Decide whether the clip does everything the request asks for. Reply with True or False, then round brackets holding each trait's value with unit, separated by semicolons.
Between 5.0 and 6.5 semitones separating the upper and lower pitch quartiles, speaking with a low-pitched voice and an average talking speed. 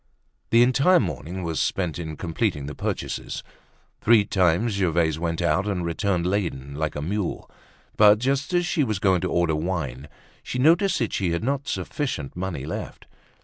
True (5.6 semitones; 90 Hz; 170 wpm)